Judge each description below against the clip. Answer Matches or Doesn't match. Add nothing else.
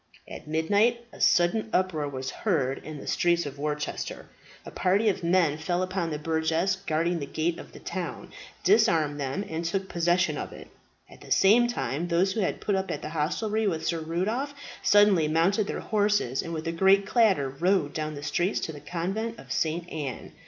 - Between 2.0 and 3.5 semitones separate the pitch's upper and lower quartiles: Doesn't match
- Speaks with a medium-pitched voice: Matches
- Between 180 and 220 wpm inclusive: Matches